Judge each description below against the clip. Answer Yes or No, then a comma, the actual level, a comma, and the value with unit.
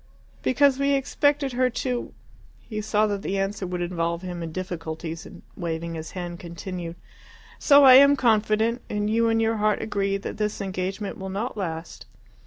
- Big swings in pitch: No, average, 4.7 semitones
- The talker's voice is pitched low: No, high, 200 Hz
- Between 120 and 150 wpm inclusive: No, average, 180 wpm